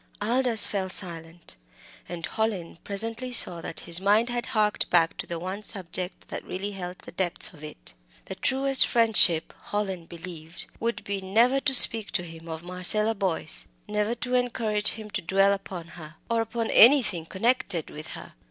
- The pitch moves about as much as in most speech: Yes, average, 4.6 semitones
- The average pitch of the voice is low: No, high, 195 Hz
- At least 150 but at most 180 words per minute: Yes, average, 170 wpm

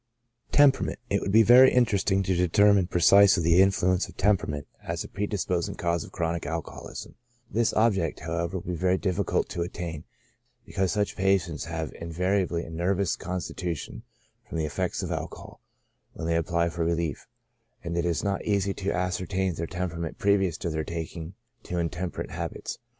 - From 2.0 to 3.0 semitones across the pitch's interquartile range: Yes, average, 2.7 semitones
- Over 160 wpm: Yes, average, 170 wpm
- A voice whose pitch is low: Yes, very low, 90 Hz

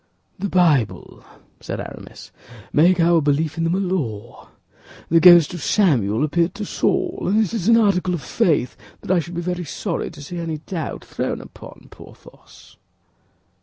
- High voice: No, medium, 170 Hz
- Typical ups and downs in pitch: Yes, average, 3.3 semitones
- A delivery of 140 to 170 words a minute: Yes, average, 165 wpm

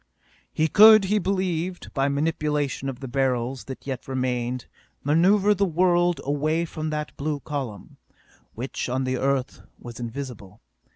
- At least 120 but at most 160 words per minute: Yes, average, 140 wpm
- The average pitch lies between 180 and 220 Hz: No, medium, 140 Hz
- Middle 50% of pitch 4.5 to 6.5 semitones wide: Yes, average, 4.8 semitones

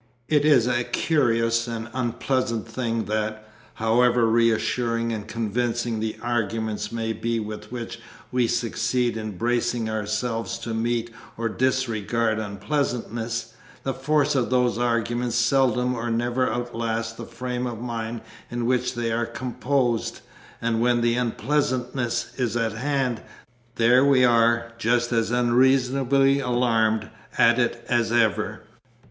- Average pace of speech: No, slow, 130 wpm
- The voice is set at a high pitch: No, low, 120 Hz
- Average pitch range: No, narrow, 1.5 semitones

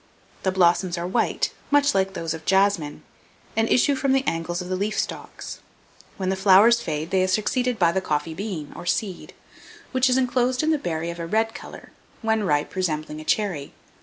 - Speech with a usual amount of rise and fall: Yes, average, 5.0 semitones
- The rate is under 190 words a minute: No, average, 195 wpm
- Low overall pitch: No, high, 190 Hz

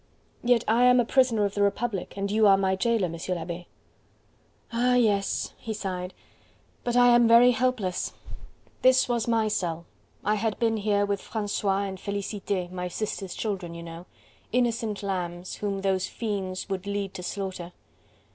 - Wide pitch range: No, average, 3.5 semitones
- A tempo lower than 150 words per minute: No, average, 165 wpm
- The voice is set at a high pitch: Yes, high, 200 Hz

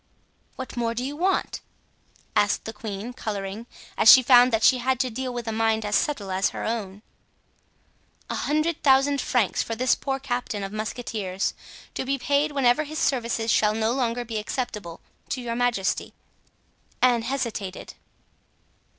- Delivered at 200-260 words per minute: No, average, 160 wpm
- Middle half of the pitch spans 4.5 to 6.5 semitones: No, average, 3.4 semitones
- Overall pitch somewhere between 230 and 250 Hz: Yes, high, 235 Hz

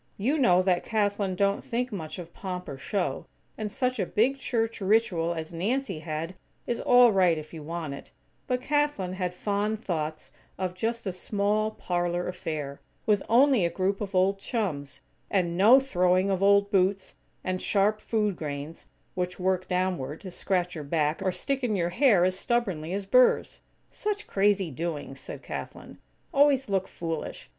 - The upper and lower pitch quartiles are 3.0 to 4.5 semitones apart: Yes, average, 3.9 semitones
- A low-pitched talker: No, high, 190 Hz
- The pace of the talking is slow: No, average, 170 wpm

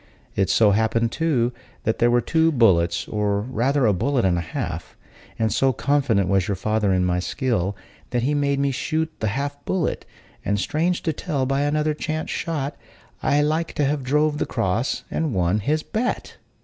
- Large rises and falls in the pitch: Yes, wide, 6.1 semitones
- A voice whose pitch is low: Yes, low, 130 Hz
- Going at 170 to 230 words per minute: Yes, average, 190 wpm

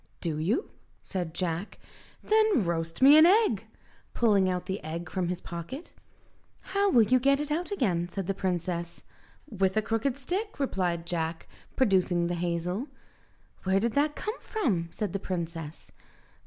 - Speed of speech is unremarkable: Yes, average, 155 wpm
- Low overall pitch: No, high, 190 Hz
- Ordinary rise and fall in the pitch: No, wide, 8.0 semitones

